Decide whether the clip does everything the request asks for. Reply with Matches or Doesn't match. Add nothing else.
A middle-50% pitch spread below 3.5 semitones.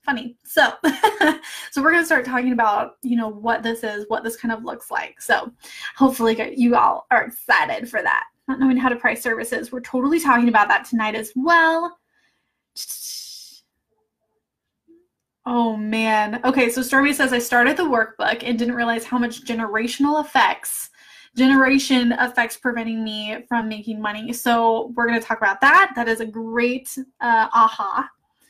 Matches